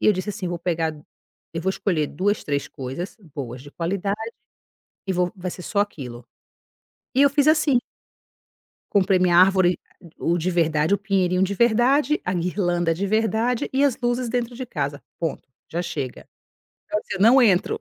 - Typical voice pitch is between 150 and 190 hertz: Yes, medium, 185 Hz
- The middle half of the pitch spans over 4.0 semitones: Yes, average, 4.7 semitones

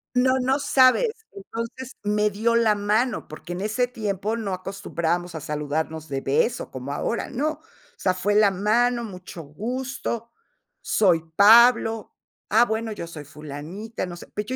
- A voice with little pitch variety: No, average, 5.0 semitones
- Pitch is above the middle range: Yes, high, 210 Hz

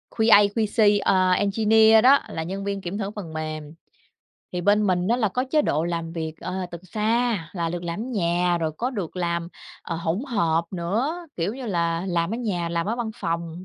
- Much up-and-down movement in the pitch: No, average, 4.4 semitones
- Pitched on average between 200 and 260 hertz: No, medium, 185 Hz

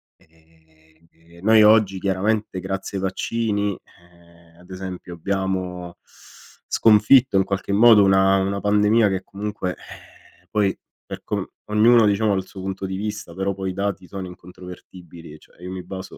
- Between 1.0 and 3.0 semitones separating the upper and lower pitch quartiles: Yes, narrow, 2.4 semitones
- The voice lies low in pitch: Yes, very low, 95 Hz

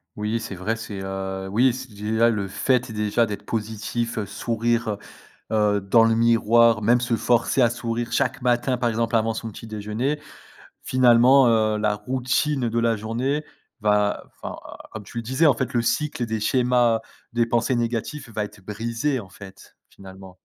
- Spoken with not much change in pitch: Yes, narrow, 2.3 semitones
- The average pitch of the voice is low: Yes, low, 115 Hz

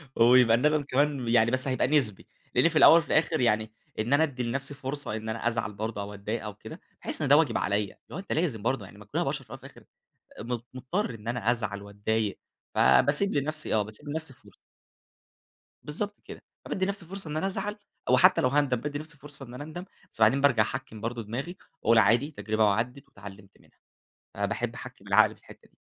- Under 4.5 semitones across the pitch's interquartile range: No, average, 5.2 semitones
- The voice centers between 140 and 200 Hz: No, low, 125 Hz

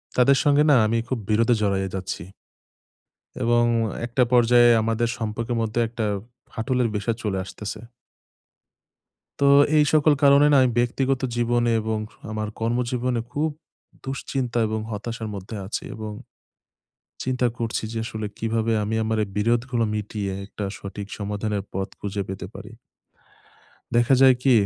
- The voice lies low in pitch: Yes, low, 115 Hz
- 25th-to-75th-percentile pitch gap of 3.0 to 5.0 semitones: No, narrow, 2.6 semitones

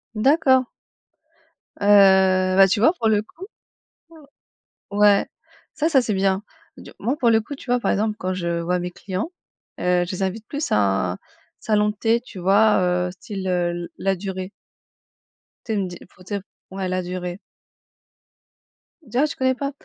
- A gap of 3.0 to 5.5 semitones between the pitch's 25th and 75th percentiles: Yes, average, 3.4 semitones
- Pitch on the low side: No, high, 195 Hz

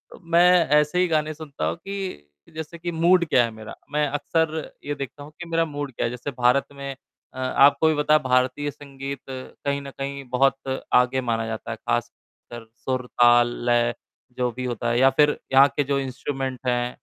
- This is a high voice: No, medium, 140 Hz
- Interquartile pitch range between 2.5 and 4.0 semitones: Yes, average, 3.2 semitones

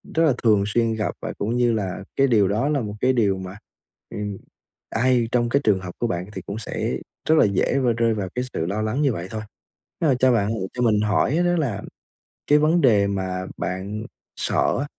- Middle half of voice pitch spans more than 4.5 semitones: No, average, 4.2 semitones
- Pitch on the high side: No, low, 110 Hz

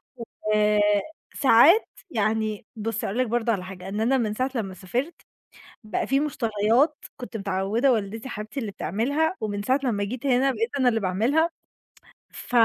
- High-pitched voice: Yes, high, 225 Hz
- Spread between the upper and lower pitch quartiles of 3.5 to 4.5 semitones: Yes, average, 3.8 semitones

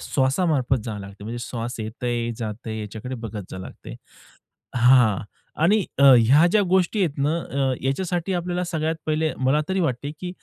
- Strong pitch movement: Yes, wide, 6.0 semitones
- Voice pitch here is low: Yes, low, 130 Hz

